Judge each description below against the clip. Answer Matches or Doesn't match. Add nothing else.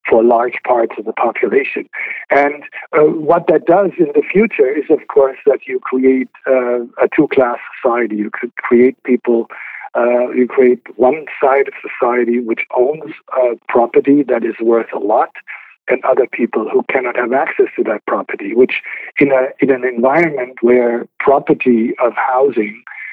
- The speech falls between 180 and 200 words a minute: Doesn't match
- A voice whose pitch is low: Matches